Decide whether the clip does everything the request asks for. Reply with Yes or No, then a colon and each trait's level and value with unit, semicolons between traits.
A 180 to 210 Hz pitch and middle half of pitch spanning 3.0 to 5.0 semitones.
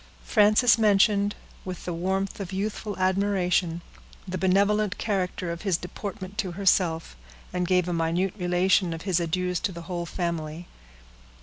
No: medium, 185 Hz; narrow, 2.4 semitones